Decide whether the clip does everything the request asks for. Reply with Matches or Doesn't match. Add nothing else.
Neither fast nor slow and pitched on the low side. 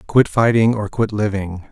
Matches